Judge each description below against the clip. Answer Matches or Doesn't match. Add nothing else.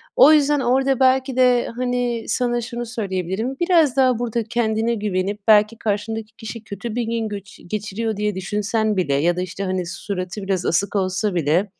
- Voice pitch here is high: Matches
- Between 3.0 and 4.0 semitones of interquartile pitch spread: Matches